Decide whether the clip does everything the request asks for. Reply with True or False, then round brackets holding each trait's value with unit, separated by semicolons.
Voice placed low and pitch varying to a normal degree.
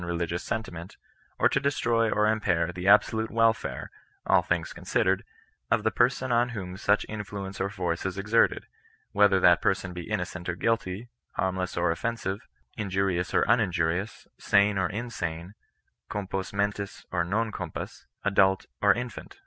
True (100 Hz; 3.5 semitones)